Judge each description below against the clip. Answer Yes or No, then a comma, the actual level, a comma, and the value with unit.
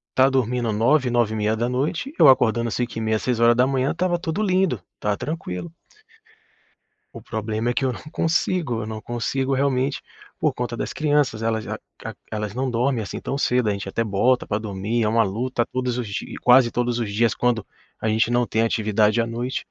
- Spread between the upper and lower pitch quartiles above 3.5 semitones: No, average, 3.0 semitones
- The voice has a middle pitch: No, low, 120 Hz